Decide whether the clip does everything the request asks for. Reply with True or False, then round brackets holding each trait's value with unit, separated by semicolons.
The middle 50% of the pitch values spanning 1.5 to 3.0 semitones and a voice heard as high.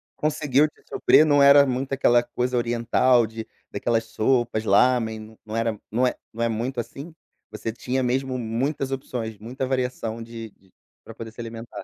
False (2.6 semitones; 120 Hz)